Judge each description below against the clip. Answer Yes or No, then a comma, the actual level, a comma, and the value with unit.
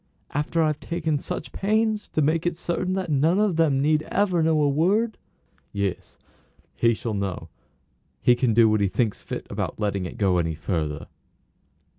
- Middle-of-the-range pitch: Yes, medium, 150 Hz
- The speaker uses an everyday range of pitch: No, wide, 8.5 semitones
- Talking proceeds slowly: No, average, 175 wpm